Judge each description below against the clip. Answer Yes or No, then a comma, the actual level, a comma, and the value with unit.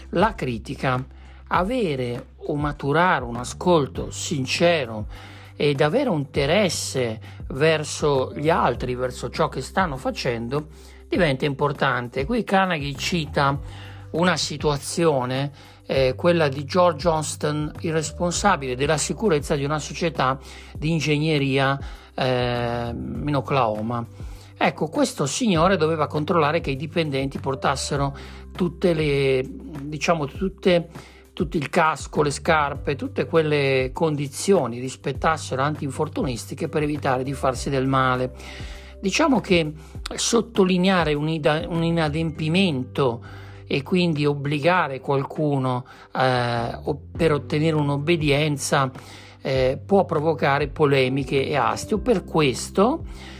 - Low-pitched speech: No, medium, 145 Hz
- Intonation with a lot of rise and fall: No, average, 4.3 semitones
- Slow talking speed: Yes, slow, 105 wpm